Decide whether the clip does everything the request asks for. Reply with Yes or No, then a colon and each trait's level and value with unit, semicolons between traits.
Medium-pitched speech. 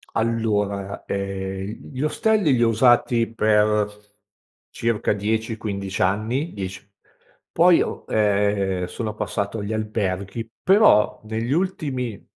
No: low, 110 Hz